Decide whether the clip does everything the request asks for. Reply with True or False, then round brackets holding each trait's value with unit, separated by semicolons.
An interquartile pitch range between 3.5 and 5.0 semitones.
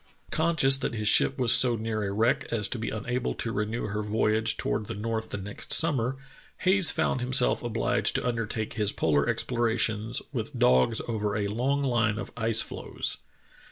False (2.7 semitones)